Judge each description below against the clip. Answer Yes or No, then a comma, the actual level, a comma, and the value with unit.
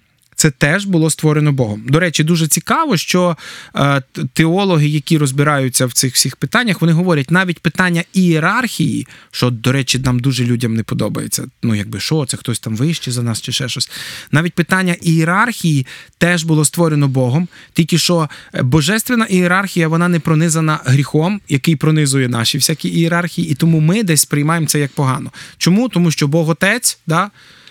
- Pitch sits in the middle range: Yes, medium, 160 Hz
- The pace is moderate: No, fast, 165 wpm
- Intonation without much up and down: No, average, 4.0 semitones